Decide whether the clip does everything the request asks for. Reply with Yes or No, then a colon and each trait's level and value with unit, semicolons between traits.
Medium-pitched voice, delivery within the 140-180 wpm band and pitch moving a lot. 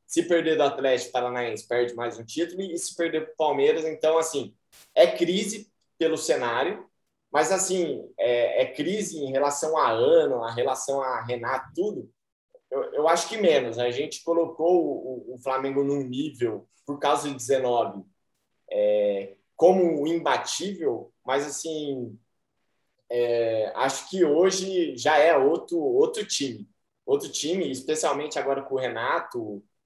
Yes: medium, 155 Hz; average, 150 wpm; wide, 6.4 semitones